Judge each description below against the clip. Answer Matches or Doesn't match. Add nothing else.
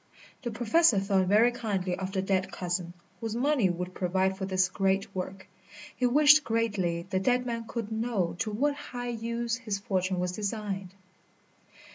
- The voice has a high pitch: Matches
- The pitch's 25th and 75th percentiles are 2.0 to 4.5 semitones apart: Matches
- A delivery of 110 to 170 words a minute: Matches